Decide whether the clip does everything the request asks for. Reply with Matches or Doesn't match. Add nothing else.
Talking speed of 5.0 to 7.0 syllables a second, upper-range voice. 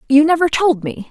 Matches